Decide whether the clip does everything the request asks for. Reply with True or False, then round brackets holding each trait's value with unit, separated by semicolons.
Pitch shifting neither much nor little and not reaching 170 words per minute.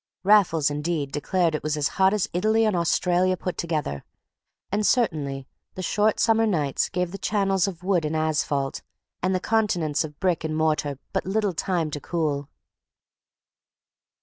True (4.2 semitones; 160 wpm)